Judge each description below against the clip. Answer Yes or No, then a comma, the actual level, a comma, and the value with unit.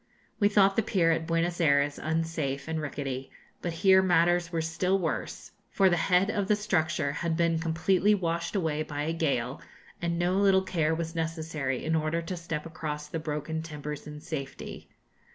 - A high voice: No, medium, 165 Hz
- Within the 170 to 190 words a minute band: Yes, average, 180 wpm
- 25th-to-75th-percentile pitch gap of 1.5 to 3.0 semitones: Yes, narrow, 2.5 semitones